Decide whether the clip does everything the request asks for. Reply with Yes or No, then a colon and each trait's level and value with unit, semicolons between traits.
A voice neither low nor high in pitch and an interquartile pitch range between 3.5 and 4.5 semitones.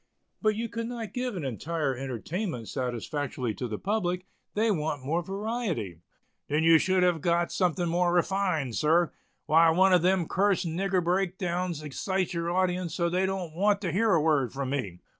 Yes: medium, 175 Hz; average, 3.9 semitones